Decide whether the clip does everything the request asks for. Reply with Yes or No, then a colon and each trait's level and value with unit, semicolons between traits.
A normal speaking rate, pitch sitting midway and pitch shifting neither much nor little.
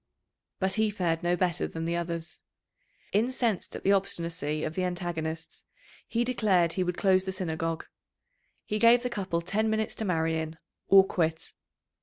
Yes: average, 165 wpm; medium, 180 Hz; average, 3.7 semitones